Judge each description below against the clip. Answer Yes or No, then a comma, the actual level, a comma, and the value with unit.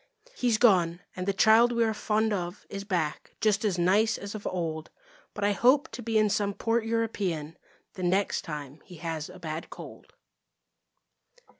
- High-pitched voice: Yes, high, 200 Hz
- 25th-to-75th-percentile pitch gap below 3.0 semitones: No, average, 4.2 semitones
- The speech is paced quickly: No, average, 175 wpm